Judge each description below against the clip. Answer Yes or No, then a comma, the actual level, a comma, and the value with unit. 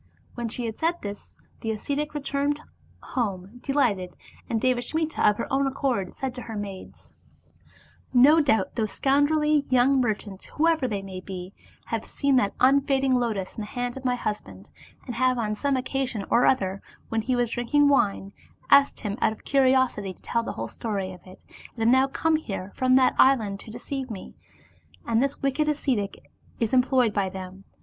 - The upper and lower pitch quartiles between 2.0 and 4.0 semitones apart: No, average, 4.6 semitones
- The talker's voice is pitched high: Yes, high, 245 Hz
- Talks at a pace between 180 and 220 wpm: Yes, average, 185 wpm